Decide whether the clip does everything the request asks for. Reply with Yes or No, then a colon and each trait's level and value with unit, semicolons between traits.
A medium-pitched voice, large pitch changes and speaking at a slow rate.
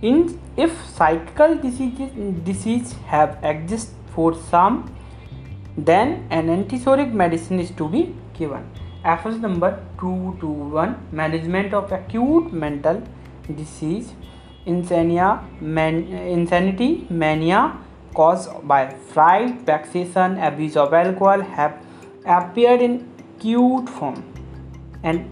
Yes: medium, 175 Hz; wide, 6.0 semitones; slow, 95 wpm